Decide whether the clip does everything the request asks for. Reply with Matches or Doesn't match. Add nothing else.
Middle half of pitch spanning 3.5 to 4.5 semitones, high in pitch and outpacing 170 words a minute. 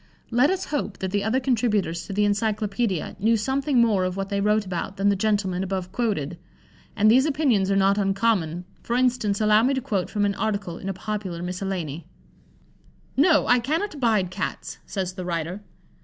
Matches